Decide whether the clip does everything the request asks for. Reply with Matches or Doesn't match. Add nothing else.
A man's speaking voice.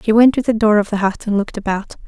Doesn't match